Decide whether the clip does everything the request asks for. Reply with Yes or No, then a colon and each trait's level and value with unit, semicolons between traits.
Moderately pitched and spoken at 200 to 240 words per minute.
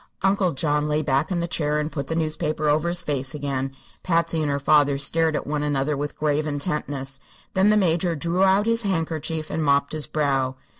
Yes: medium, 150 Hz; fast, 205 wpm